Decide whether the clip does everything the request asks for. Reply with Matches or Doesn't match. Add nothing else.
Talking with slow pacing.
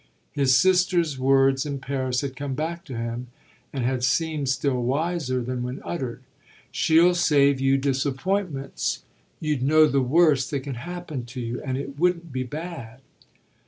Doesn't match